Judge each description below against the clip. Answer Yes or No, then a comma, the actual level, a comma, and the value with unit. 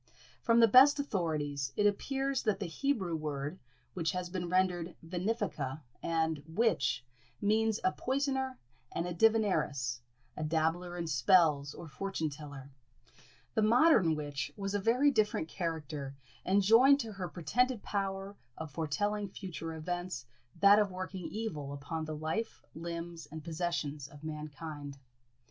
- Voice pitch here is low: No, medium, 175 Hz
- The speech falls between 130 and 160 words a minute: Yes, average, 140 wpm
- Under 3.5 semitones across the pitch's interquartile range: No, average, 5.2 semitones